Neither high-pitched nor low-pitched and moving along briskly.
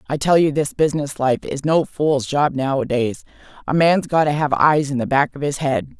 Yes: medium, 145 Hz; fast, 220 wpm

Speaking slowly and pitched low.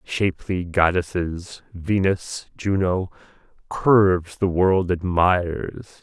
Yes: slow, 80 wpm; very low, 90 Hz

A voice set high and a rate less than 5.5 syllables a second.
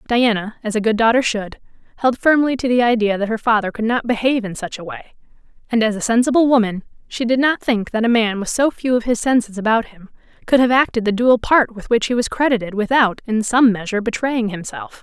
No: high, 230 Hz; 6.0 syllables/s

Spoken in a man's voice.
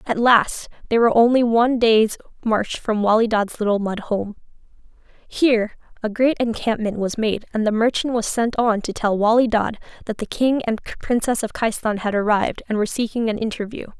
No: female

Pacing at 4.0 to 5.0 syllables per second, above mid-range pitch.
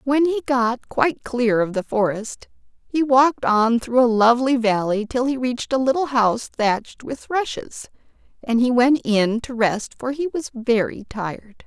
Yes: 4.6 syllables/s; high, 245 Hz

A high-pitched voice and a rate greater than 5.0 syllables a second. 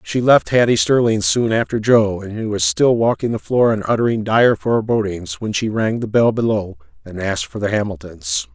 No: low, 110 Hz; 5.2 syllables/s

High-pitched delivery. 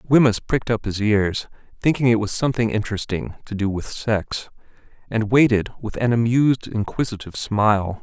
No: low, 110 Hz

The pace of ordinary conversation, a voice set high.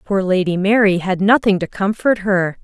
Yes: average, 180 wpm; high, 195 Hz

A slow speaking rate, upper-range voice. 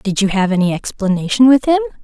No: fast, 205 wpm; high, 215 Hz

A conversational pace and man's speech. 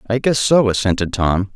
Yes: average, 195 wpm; male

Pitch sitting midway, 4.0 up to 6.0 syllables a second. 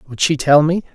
Yes: medium, 150 Hz; 4.9 syllables/s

